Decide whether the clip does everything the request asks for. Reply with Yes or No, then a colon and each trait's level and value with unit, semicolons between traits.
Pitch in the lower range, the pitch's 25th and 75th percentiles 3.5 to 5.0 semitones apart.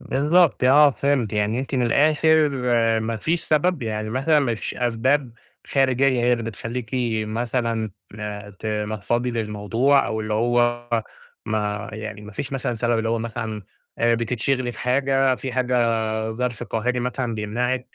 No: low, 120 Hz; average, 3.0 semitones